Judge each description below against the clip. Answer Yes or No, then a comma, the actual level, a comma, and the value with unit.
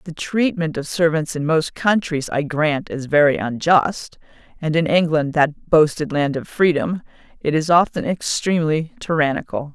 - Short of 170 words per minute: Yes, average, 155 wpm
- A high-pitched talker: No, medium, 160 Hz